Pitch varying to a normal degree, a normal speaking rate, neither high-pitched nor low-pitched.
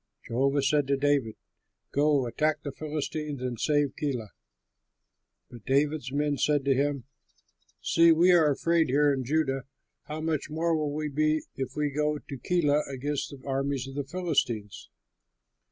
No: narrow, 2.2 semitones; average, 155 wpm; medium, 145 Hz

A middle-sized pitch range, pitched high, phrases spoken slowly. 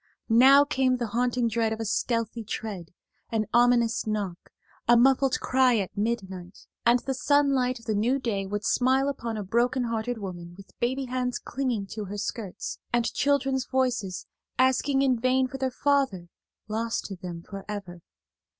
No: average, 3.8 semitones; high, 235 Hz; average, 165 wpm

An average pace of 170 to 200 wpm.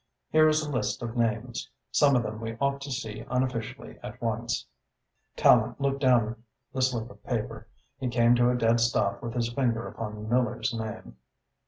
Yes: average, 180 wpm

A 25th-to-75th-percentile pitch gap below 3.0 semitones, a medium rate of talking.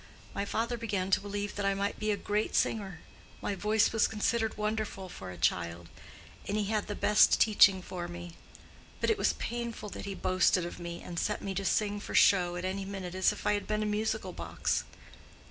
No: narrow, 2.5 semitones; fast, 215 wpm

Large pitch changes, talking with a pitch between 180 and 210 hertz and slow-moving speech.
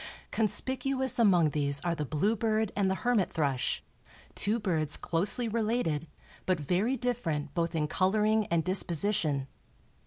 Yes: wide, 5.9 semitones; high, 190 Hz; slow, 130 wpm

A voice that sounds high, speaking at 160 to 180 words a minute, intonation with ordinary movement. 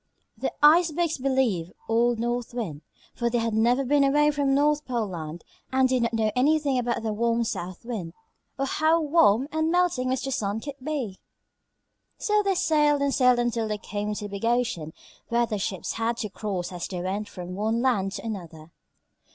No: high, 235 Hz; average, 190 wpm; average, 4.9 semitones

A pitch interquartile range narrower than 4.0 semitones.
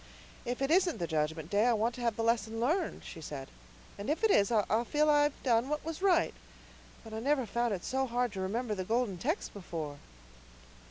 No: wide, 5.6 semitones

